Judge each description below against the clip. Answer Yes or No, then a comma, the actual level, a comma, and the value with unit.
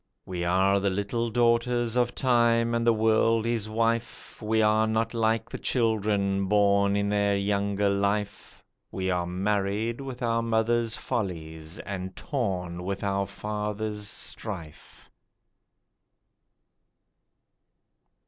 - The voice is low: Yes, low, 105 Hz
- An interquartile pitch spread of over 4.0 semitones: No, average, 2.7 semitones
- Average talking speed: No, slow, 120 wpm